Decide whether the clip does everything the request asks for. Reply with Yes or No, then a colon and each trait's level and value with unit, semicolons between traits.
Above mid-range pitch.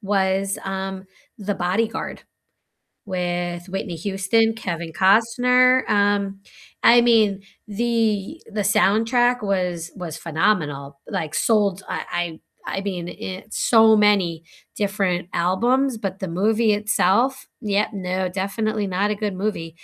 Yes: high, 195 Hz